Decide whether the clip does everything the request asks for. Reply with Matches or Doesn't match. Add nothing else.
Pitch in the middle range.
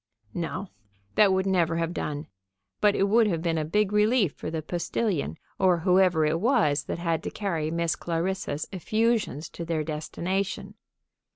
Matches